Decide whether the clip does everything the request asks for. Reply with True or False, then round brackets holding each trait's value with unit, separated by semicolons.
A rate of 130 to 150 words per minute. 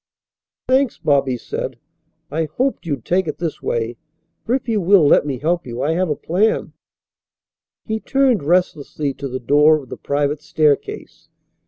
False (160 wpm)